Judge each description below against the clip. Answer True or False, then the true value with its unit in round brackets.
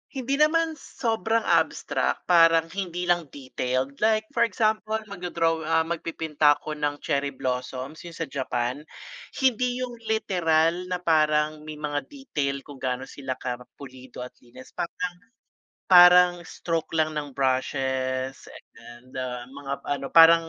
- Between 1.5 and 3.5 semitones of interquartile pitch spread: False (5.2 semitones)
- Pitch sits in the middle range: True (155 Hz)